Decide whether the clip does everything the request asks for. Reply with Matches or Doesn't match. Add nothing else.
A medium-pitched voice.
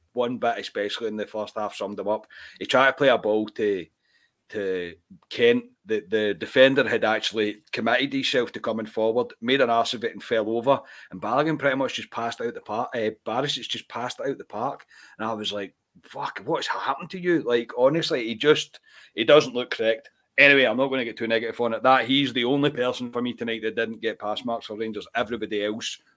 Doesn't match